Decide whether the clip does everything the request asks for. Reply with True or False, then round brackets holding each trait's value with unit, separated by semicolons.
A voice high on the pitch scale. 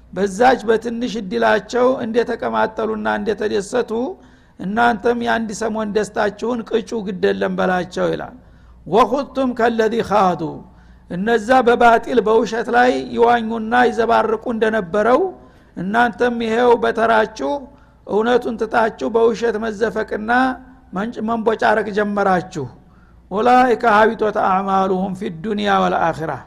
True (225 Hz)